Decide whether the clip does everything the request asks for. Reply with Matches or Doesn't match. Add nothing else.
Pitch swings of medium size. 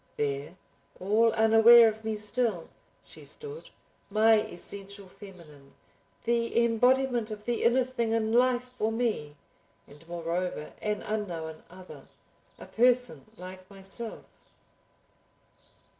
Matches